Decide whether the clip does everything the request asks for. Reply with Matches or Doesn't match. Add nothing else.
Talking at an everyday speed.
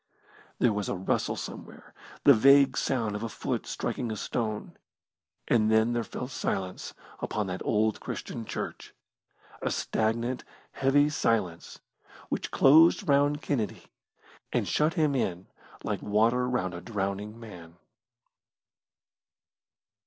Doesn't match